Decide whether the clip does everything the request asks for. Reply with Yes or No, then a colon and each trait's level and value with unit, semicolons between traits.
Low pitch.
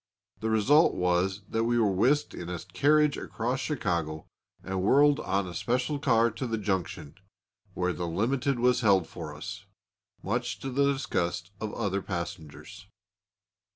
Yes: low, 105 Hz